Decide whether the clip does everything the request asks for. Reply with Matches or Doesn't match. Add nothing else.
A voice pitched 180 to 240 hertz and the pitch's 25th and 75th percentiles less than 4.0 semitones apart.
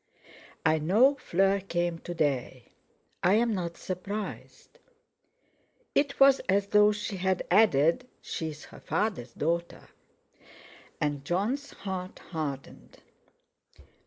Doesn't match